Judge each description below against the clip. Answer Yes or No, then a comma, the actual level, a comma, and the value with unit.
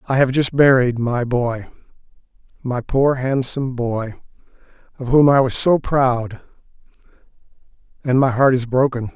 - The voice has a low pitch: Yes, low, 125 Hz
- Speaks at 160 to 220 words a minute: No, average, 140 wpm